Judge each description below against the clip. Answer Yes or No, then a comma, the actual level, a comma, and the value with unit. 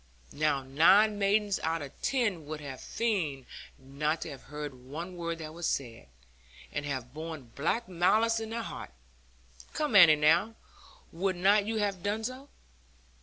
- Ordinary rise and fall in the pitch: No, wide, 6.0 semitones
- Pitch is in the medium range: Yes, medium, 170 Hz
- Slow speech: No, average, 160 wpm